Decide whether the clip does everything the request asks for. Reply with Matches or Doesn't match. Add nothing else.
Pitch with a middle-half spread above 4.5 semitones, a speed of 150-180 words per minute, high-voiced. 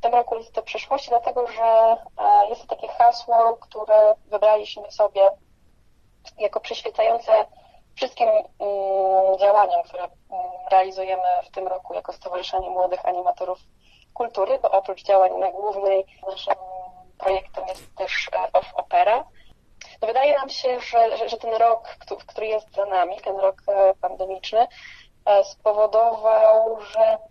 Doesn't match